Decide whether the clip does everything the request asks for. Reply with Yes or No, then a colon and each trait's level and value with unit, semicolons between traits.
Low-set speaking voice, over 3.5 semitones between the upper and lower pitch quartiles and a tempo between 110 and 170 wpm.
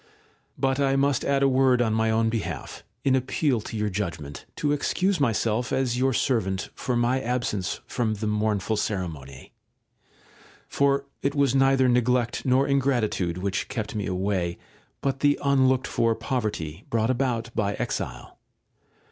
Yes: low, 120 Hz; average, 4.1 semitones; average, 155 wpm